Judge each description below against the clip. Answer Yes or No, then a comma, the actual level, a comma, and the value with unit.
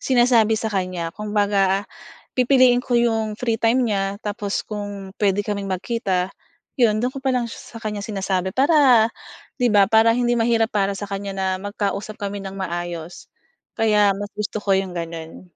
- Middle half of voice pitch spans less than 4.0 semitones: Yes, average, 2.8 semitones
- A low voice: No, high, 205 Hz